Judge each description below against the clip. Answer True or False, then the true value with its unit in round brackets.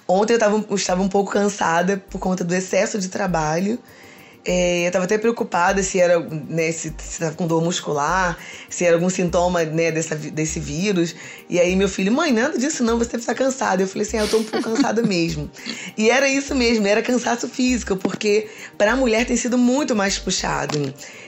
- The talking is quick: True (205 wpm)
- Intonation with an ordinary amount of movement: True (4.6 semitones)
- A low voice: False (195 Hz)